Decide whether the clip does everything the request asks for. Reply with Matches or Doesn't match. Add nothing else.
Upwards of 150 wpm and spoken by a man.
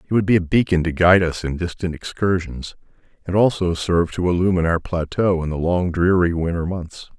Matches